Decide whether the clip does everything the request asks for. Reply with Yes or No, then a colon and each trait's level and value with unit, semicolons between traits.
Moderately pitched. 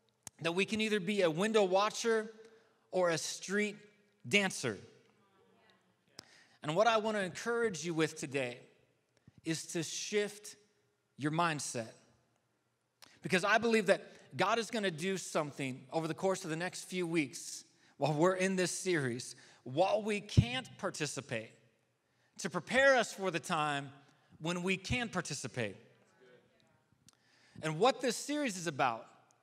Yes: medium, 180 Hz